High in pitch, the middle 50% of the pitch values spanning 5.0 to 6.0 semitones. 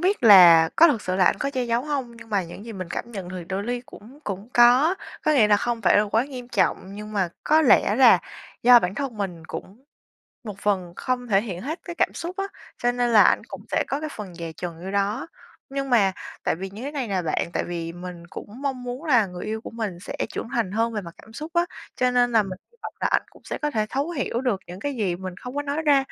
Yes: high, 225 Hz; average, 5.3 semitones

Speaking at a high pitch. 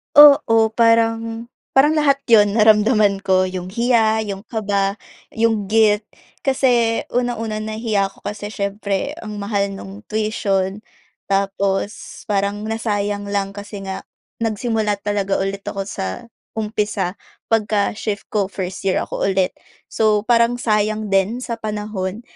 Yes: high, 210 Hz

